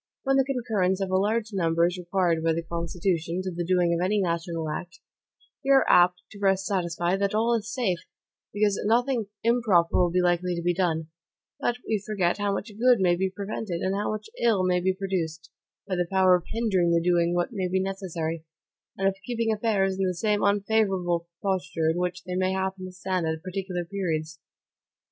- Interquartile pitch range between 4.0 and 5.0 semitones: No, average, 2.7 semitones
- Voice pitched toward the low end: No, medium, 185 Hz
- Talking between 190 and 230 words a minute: Yes, average, 200 wpm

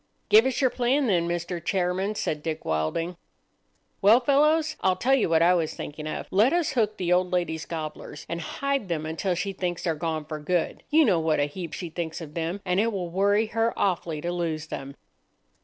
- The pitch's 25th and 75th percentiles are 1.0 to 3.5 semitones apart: No, average, 4.7 semitones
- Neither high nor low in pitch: Yes, medium, 175 Hz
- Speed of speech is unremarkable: No, fast, 210 wpm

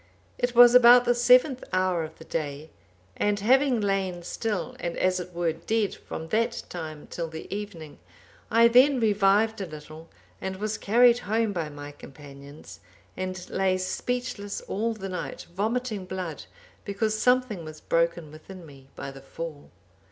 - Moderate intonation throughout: No, wide, 5.7 semitones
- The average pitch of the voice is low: No, high, 190 Hz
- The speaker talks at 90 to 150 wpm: No, average, 160 wpm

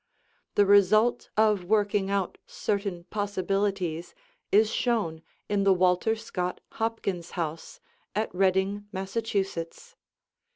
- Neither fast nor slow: No, slow, 100 wpm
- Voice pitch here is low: No, high, 200 Hz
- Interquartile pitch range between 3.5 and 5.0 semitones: No, average, 2.7 semitones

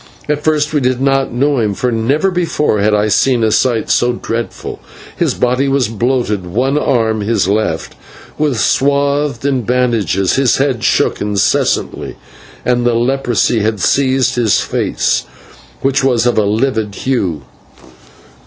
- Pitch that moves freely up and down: No, average, 3.8 semitones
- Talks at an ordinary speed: Yes, average, 150 wpm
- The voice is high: No, low, 125 Hz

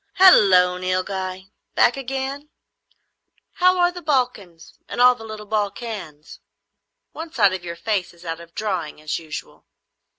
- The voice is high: Yes, high, 205 Hz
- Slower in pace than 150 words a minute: Yes, average, 140 wpm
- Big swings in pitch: Yes, wide, 6.5 semitones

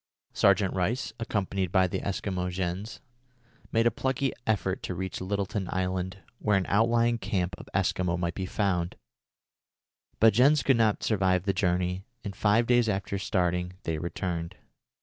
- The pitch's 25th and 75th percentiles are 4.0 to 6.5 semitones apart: No, average, 3.0 semitones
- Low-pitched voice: Yes, very low, 95 Hz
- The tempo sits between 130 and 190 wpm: Yes, average, 150 wpm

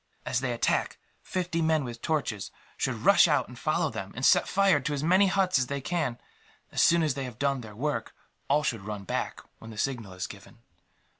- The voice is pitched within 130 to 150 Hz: Yes, low, 135 Hz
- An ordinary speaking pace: No, fast, 215 wpm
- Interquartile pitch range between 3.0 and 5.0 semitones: No, wide, 5.5 semitones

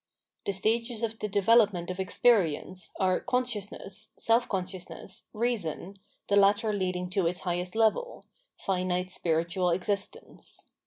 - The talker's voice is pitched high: Yes, high, 195 Hz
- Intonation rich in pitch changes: No, average, 3.5 semitones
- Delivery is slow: Yes, slow, 125 wpm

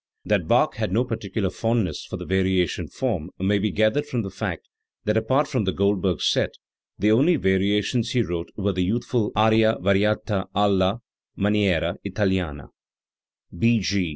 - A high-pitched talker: No, low, 105 Hz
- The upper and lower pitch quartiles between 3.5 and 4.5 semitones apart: No, average, 3.0 semitones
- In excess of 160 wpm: No, average, 155 wpm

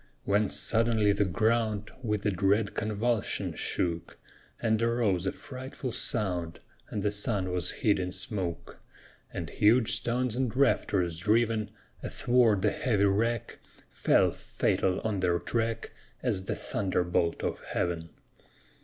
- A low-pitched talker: Yes, low, 105 Hz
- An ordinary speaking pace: No, slow, 130 wpm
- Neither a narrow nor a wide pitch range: Yes, average, 3.6 semitones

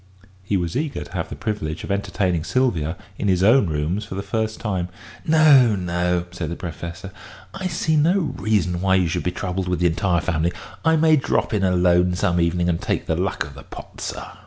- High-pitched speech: No, very low, 90 Hz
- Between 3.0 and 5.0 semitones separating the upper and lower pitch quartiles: Yes, average, 3.8 semitones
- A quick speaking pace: Yes, fast, 210 wpm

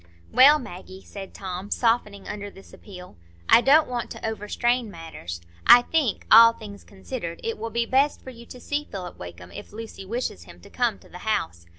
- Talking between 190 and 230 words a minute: Yes, average, 195 wpm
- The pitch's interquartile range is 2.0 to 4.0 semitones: No, average, 4.6 semitones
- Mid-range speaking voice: No, high, 210 Hz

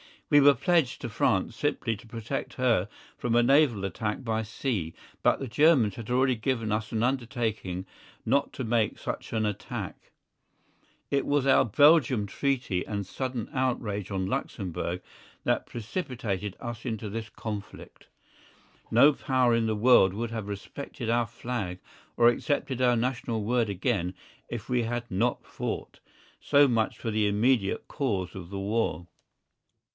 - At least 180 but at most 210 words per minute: No, average, 155 wpm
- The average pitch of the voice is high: No, low, 115 Hz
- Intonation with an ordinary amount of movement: Yes, average, 3.6 semitones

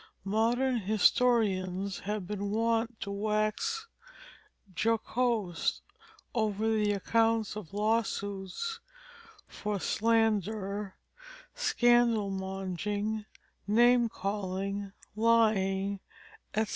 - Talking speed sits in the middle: No, slow, 80 wpm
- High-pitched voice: Yes, high, 215 Hz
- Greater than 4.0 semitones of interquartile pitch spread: No, narrow, 2.4 semitones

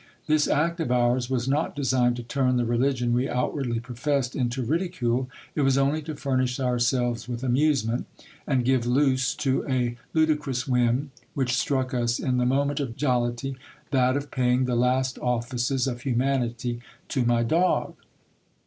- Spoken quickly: No, average, 160 wpm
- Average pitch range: No, narrow, 2.1 semitones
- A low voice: Yes, low, 125 Hz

